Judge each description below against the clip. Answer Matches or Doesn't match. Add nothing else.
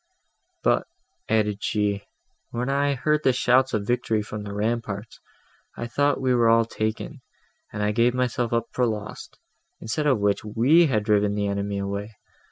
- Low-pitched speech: Matches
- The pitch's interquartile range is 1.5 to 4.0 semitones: Matches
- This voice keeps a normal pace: Matches